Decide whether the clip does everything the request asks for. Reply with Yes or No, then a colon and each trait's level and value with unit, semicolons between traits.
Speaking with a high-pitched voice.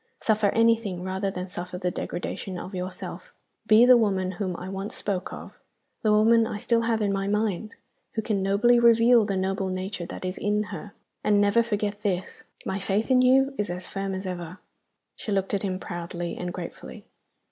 Yes: high, 200 Hz